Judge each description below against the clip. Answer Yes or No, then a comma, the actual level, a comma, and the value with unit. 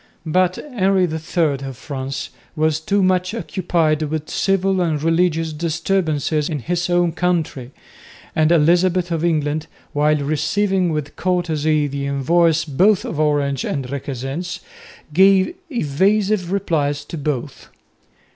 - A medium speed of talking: No, slow, 125 wpm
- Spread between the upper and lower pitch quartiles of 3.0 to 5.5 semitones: Yes, average, 3.6 semitones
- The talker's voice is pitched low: No, medium, 160 Hz